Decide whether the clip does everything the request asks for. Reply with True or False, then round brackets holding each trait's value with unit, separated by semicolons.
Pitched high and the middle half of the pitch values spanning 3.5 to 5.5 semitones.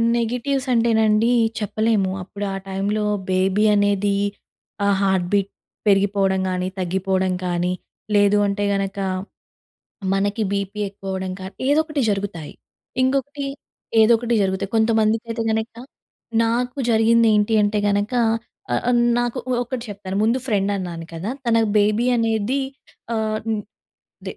False (205 Hz; 2.8 semitones)